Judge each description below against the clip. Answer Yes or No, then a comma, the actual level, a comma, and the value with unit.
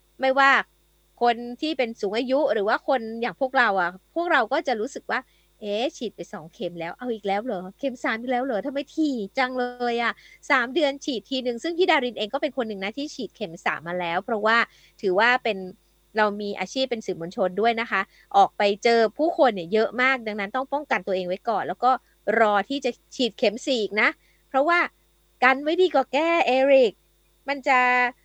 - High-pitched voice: Yes, high, 245 Hz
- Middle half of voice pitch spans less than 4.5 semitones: No, average, 5.0 semitones